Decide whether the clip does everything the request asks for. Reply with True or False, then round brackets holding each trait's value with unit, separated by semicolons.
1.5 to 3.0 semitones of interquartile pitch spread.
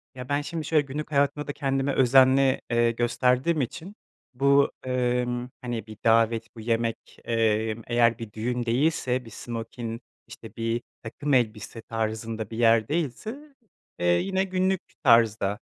False (3.5 semitones)